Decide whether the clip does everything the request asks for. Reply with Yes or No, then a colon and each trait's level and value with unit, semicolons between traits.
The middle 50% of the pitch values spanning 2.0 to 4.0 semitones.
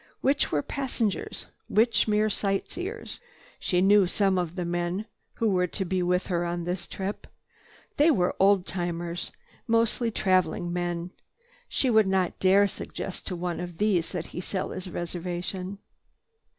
Yes: average, 2.9 semitones